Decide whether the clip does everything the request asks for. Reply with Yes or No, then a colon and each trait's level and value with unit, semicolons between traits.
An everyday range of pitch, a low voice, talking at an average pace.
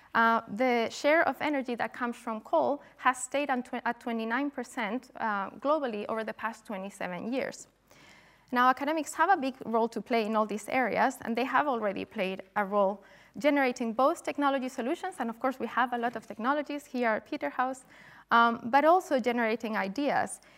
No: average, 3.5 semitones; high, 245 Hz; average, 180 wpm